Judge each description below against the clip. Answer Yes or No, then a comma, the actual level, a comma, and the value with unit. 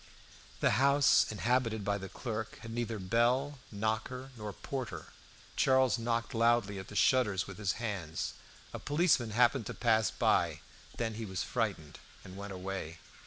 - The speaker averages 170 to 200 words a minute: No, average, 155 wpm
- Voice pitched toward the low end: Yes, low, 110 Hz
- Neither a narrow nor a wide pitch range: Yes, average, 3.4 semitones